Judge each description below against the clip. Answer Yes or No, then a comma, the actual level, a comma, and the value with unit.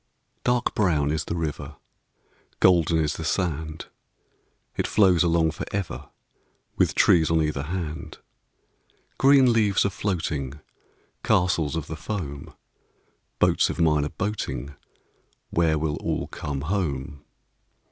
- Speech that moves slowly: Yes, slow, 125 wpm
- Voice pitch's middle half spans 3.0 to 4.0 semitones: Yes, average, 3.6 semitones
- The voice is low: Yes, very low, 80 Hz